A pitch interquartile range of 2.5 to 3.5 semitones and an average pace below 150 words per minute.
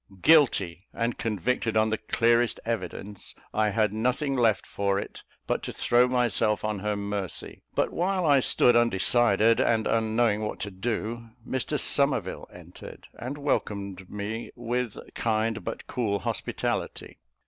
Yes: average, 2.8 semitones; average, 140 wpm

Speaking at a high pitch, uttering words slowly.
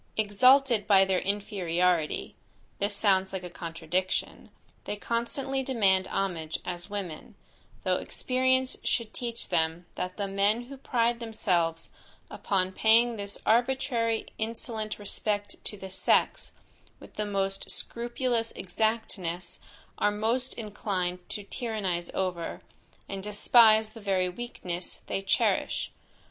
Yes: high, 205 Hz; slow, 120 wpm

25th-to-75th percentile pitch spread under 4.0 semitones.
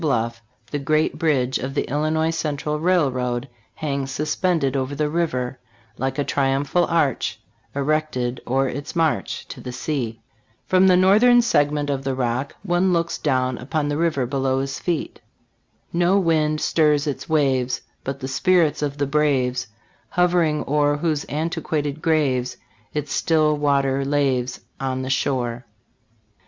Yes: average, 3.0 semitones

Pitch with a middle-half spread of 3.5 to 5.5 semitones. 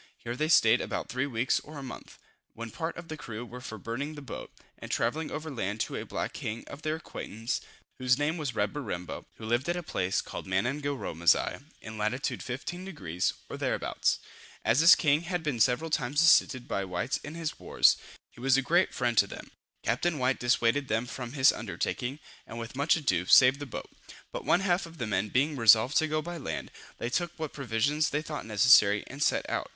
Yes: average, 5.2 semitones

